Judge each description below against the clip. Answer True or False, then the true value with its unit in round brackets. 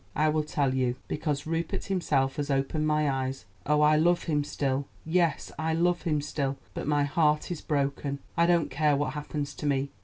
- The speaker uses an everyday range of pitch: False (2.1 semitones)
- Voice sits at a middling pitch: True (150 Hz)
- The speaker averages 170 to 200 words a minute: True (195 wpm)